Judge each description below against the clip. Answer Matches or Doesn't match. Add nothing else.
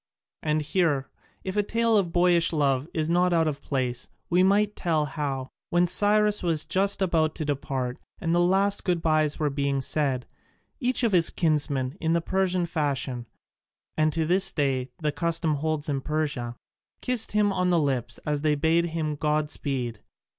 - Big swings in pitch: Doesn't match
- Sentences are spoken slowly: Doesn't match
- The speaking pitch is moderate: Matches